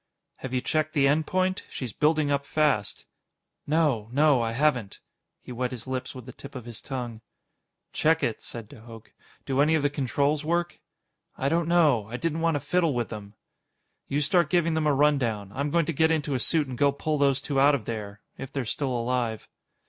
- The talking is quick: Yes, fast, 210 wpm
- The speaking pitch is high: No, medium, 140 Hz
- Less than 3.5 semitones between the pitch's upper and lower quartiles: No, average, 4.1 semitones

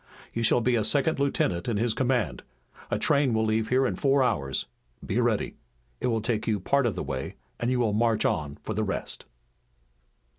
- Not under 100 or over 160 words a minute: No, average, 200 wpm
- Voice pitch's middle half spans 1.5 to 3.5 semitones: Yes, average, 3.1 semitones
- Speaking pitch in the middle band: No, low, 115 Hz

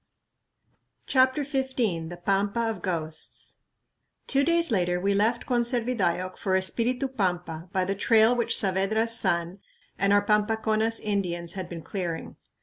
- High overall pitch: Yes, high, 200 Hz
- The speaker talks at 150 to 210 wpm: No, slow, 135 wpm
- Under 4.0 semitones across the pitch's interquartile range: No, average, 4.4 semitones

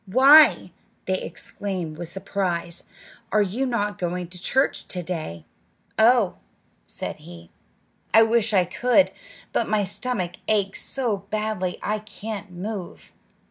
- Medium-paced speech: No, slow, 130 wpm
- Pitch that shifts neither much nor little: Yes, average, 3.7 semitones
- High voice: Yes, high, 200 Hz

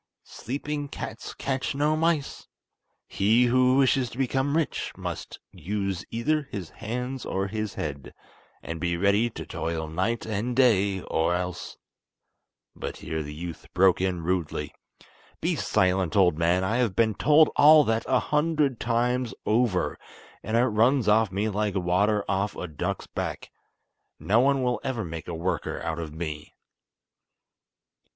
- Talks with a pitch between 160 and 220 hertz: No, low, 105 Hz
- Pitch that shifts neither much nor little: No, wide, 5.9 semitones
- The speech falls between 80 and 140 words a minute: No, average, 150 wpm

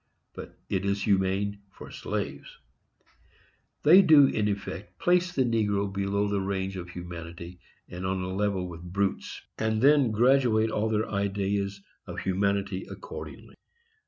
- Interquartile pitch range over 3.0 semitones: No, narrow, 2.4 semitones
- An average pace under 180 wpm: Yes, average, 140 wpm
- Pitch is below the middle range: Yes, low, 100 Hz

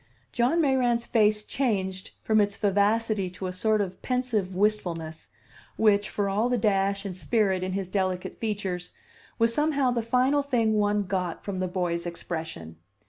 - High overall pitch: Yes, high, 205 Hz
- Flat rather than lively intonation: No, average, 3.6 semitones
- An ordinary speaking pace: Yes, average, 160 wpm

